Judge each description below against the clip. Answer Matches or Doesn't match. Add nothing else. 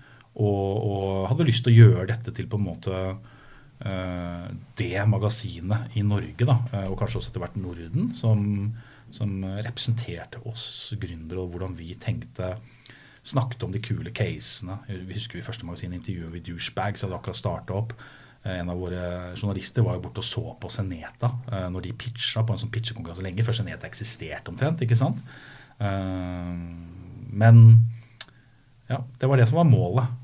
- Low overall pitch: Matches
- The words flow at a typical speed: Matches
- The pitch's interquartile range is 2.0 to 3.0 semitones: Doesn't match